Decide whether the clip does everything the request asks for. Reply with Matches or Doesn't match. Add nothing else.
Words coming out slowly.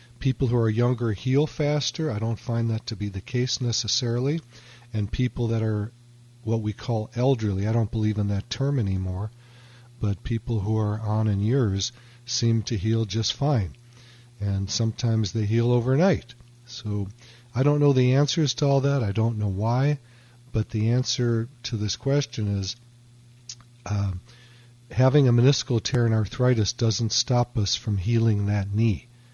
Doesn't match